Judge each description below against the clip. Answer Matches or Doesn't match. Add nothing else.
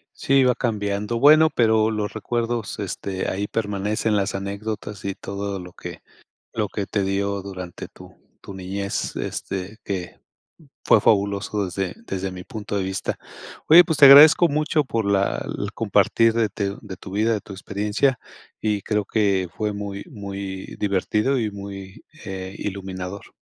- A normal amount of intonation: Doesn't match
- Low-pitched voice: Matches